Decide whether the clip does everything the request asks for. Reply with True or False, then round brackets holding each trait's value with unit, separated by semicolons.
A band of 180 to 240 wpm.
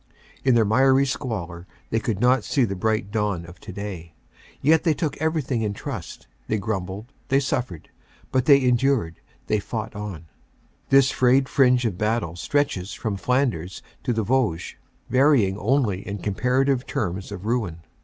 False (160 wpm)